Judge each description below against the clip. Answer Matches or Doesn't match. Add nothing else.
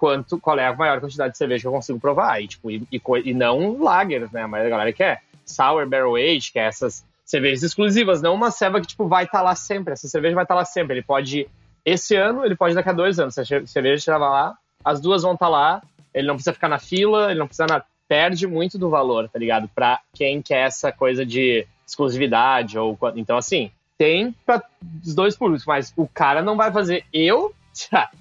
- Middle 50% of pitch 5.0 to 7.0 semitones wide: Matches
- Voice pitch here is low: Doesn't match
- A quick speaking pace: Matches